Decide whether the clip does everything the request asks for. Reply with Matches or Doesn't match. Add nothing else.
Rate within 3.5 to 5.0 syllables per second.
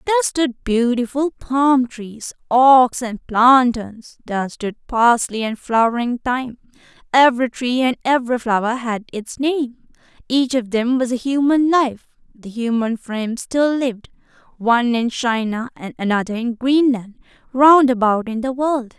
Matches